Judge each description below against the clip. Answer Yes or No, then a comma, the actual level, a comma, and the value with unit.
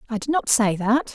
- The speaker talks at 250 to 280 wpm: Yes, fast, 260 wpm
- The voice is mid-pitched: No, high, 230 Hz